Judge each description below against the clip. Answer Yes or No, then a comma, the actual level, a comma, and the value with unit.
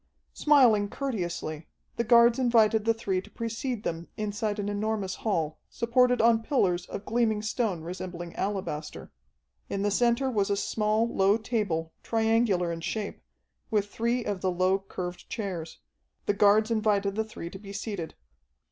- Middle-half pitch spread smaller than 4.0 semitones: Yes, average, 3.4 semitones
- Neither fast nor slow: Yes, average, 155 wpm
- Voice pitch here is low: No, high, 210 Hz